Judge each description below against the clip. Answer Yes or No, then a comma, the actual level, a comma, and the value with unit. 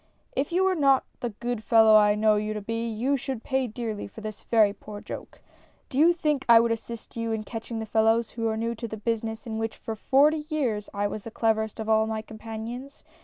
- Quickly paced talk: Yes, fast, 235 wpm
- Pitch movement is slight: Yes, narrow, 2.0 semitones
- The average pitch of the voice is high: Yes, high, 225 Hz